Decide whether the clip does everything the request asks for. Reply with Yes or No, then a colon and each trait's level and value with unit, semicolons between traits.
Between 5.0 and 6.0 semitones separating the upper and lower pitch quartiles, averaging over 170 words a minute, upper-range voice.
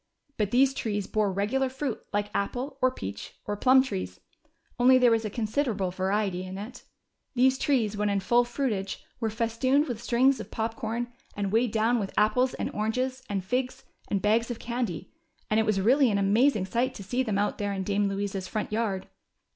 No: average, 3.8 semitones; average, 195 wpm; high, 220 Hz